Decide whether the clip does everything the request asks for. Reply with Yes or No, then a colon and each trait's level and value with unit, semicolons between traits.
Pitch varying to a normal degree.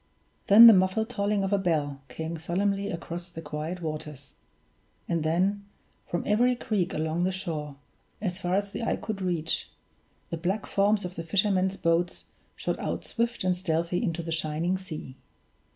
Yes: average, 3.5 semitones